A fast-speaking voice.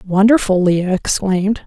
No: slow, 110 wpm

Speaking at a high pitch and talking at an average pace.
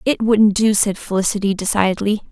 Yes: high, 205 Hz; average, 155 wpm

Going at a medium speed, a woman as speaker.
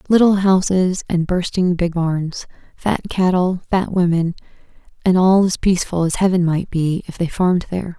Yes: average, 165 wpm; female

